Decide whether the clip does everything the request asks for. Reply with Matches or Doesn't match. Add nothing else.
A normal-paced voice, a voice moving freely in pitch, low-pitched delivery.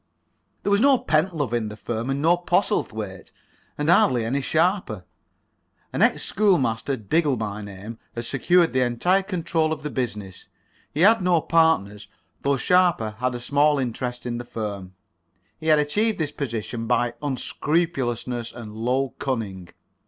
Matches